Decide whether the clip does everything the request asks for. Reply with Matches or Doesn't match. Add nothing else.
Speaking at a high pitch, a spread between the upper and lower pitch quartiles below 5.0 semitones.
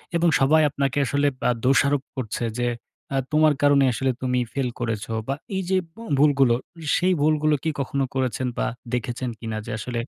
Doesn't match